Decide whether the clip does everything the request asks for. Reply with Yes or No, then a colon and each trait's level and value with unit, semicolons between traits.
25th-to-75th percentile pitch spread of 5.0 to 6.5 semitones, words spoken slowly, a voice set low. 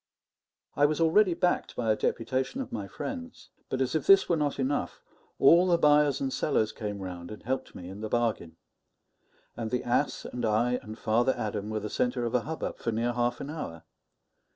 No: average, 5.3 semitones; average, 200 wpm; low, 120 Hz